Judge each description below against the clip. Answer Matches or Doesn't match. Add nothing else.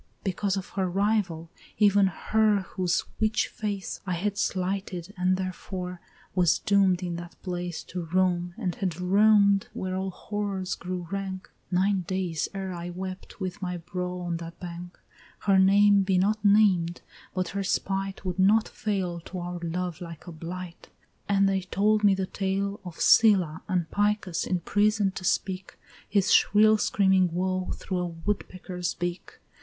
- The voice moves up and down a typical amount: Doesn't match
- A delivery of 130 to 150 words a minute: Doesn't match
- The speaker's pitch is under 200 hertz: Matches